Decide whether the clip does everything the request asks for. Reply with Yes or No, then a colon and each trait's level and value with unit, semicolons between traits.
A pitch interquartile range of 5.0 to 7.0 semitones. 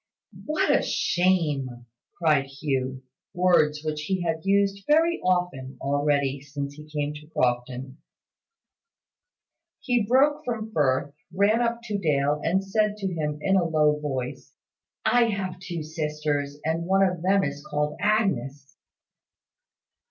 Yes: wide, 5.4 semitones